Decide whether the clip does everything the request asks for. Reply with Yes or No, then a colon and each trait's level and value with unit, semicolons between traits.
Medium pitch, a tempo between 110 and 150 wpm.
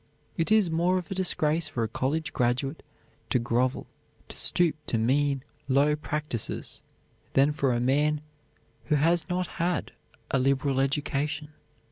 Yes: medium, 145 Hz; average, 145 wpm